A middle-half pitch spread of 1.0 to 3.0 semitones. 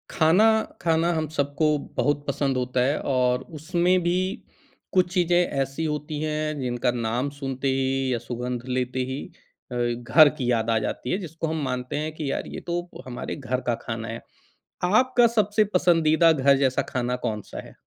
No: average, 4.3 semitones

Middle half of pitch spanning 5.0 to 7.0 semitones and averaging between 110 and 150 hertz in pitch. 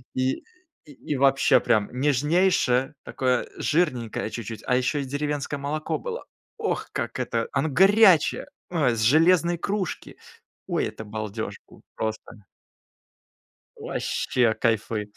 Yes: wide, 5.4 semitones; low, 135 Hz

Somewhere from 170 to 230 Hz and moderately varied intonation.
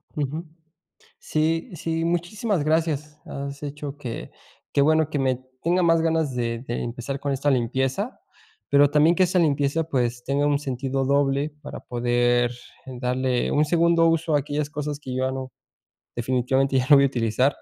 No: medium, 140 Hz; average, 3.3 semitones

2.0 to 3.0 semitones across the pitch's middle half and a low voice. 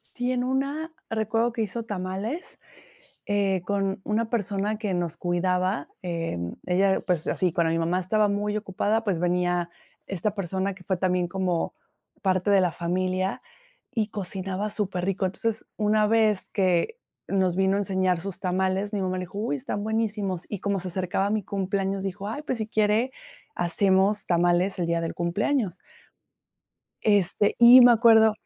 No: average, 2.7 semitones; high, 195 Hz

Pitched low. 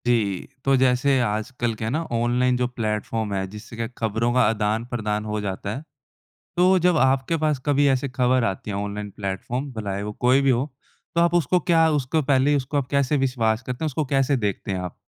Yes: low, 125 Hz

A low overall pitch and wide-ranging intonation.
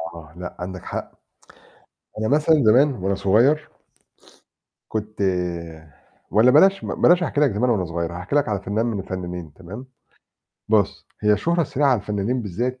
Yes: low, 110 Hz; wide, 6.0 semitones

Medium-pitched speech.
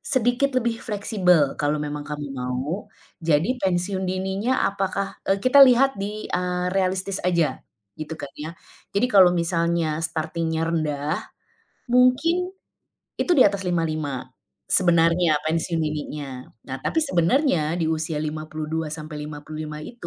Yes: medium, 170 Hz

